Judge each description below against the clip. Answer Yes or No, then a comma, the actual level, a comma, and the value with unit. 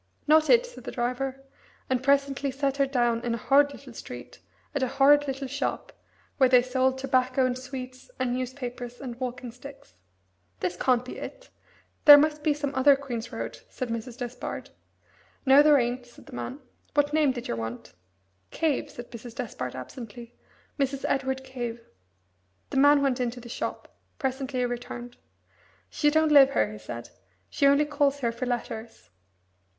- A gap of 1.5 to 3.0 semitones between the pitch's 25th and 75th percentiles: Yes, narrow, 2.6 semitones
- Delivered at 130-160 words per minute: No, average, 170 wpm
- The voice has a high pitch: Yes, very high, 260 Hz